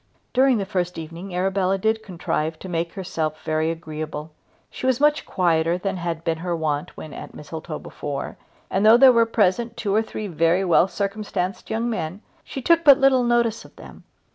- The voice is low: No, medium, 185 Hz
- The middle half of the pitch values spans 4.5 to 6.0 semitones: Yes, average, 5.3 semitones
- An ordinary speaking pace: Yes, average, 190 wpm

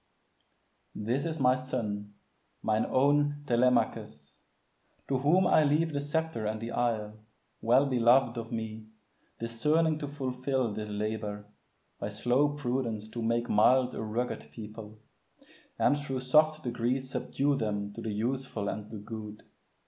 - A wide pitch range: No, average, 4.2 semitones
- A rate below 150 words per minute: Yes, average, 140 wpm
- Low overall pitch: Yes, low, 120 Hz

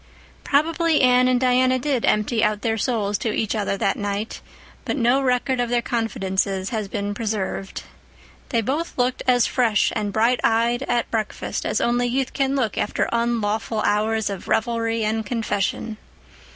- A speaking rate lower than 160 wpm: No, average, 165 wpm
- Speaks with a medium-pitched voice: No, high, 230 Hz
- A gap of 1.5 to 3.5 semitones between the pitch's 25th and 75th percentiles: Yes, average, 2.9 semitones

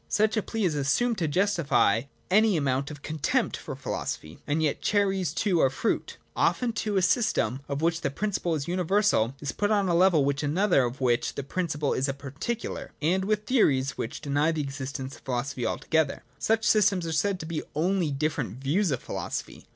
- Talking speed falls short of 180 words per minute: No, average, 200 wpm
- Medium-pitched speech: Yes, medium, 160 Hz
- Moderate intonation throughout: No, wide, 6.1 semitones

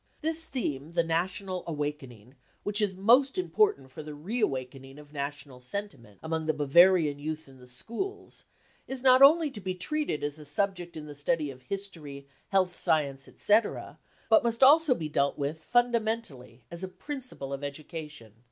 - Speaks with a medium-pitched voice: Yes, medium, 160 Hz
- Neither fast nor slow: Yes, average, 170 wpm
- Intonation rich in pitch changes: Yes, wide, 7.4 semitones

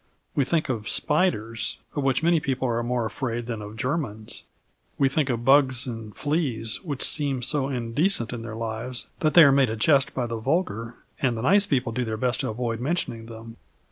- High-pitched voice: No, low, 125 Hz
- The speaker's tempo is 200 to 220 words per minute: Yes, fast, 205 wpm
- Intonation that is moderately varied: Yes, average, 3.7 semitones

